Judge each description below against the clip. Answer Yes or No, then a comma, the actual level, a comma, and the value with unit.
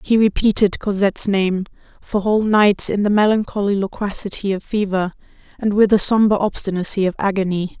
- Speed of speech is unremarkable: Yes, average, 155 wpm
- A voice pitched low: No, high, 200 Hz